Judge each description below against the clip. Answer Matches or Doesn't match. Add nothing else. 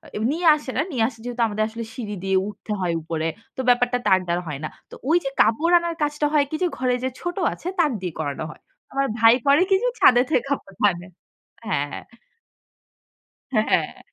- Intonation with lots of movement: Matches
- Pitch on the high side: Matches